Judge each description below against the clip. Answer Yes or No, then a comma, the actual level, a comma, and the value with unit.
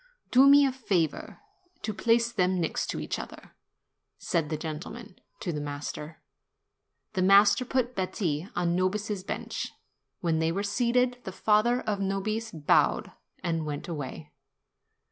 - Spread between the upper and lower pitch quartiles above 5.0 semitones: Yes, wide, 5.6 semitones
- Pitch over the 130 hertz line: Yes, high, 190 Hz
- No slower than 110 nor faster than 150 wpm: Yes, average, 140 wpm